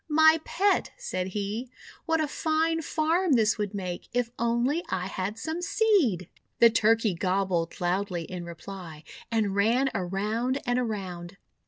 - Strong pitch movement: Yes, wide, 8.0 semitones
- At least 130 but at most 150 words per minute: Yes, average, 145 wpm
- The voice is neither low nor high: No, high, 220 Hz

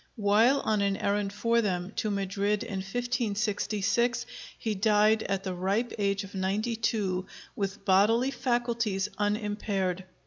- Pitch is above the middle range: Yes, high, 205 Hz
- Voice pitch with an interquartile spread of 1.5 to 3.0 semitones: Yes, narrow, 2.5 semitones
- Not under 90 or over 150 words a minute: Yes, slow, 135 wpm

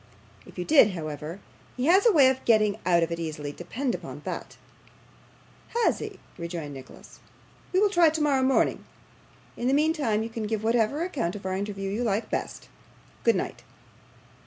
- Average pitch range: No, wide, 7.8 semitones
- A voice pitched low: No, high, 220 Hz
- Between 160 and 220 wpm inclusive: Yes, average, 175 wpm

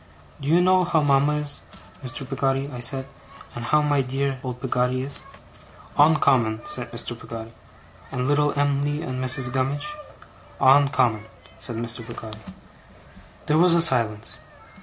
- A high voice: No, low, 135 Hz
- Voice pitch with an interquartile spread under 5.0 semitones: Yes, average, 3.1 semitones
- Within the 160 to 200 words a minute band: No, average, 150 wpm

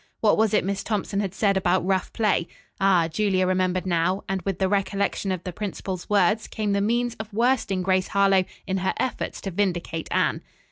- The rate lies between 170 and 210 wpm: Yes, average, 195 wpm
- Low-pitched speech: No, high, 195 Hz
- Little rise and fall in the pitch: Yes, narrow, 1.9 semitones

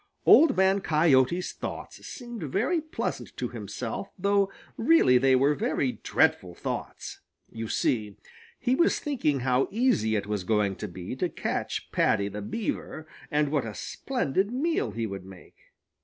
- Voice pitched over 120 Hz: Yes, medium, 140 Hz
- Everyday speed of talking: Yes, average, 155 wpm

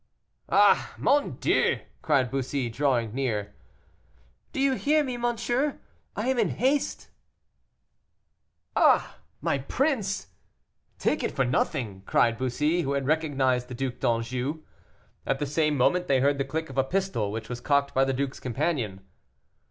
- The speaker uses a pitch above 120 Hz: Yes, medium, 140 Hz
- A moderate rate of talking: Yes, average, 150 wpm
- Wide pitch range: Yes, wide, 5.9 semitones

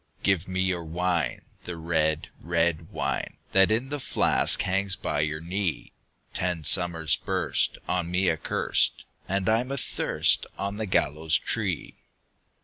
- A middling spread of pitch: Yes, average, 3.1 semitones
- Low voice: Yes, very low, 90 Hz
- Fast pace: No, average, 140 wpm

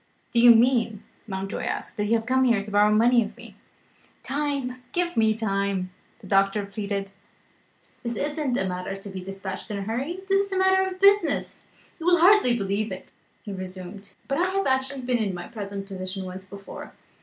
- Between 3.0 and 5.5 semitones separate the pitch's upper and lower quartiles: Yes, average, 5.2 semitones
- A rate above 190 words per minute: Yes, average, 200 wpm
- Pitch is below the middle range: No, high, 220 Hz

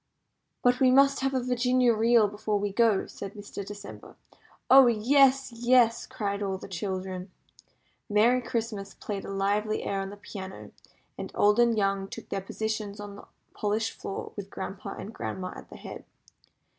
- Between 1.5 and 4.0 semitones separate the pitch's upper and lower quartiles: Yes, average, 3.2 semitones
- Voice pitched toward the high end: Yes, high, 210 Hz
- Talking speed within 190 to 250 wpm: No, average, 170 wpm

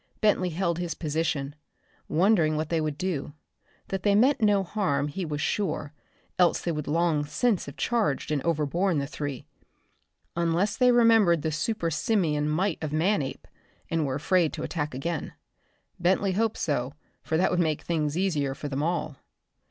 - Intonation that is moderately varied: Yes, average, 4.2 semitones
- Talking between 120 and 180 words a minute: Yes, average, 165 wpm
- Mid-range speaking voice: Yes, medium, 165 Hz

